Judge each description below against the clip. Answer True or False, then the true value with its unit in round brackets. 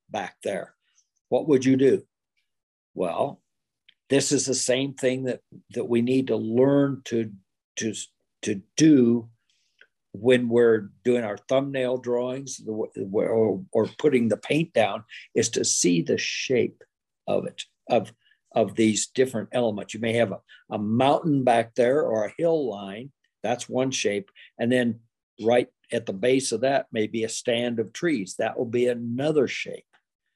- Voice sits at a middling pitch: False (120 Hz)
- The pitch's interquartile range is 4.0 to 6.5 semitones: False (2.8 semitones)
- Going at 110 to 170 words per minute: True (160 wpm)